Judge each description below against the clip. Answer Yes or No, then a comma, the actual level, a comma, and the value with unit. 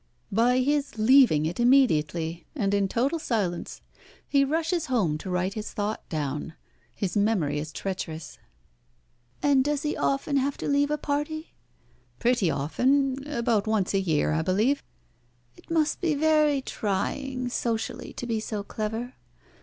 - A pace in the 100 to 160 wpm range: Yes, average, 145 wpm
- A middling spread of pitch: No, wide, 6.8 semitones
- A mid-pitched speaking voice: No, high, 235 Hz